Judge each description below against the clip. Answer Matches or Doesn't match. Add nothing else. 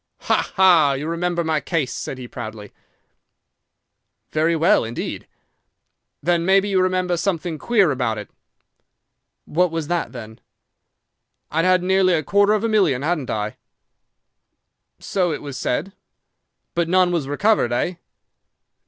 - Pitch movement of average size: Matches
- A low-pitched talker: Doesn't match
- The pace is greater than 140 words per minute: Doesn't match